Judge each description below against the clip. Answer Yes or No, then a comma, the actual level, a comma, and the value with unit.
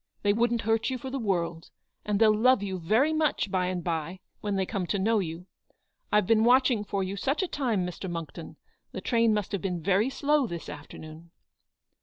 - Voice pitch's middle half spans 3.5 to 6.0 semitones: Yes, average, 4.6 semitones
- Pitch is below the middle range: No, high, 205 Hz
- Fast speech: Yes, fast, 210 wpm